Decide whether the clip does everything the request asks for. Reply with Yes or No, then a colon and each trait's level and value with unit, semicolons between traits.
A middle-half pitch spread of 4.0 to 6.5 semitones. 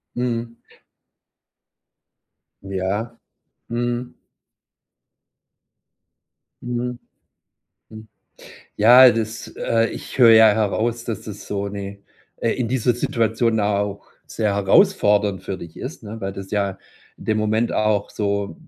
No: narrow, 2.5 semitones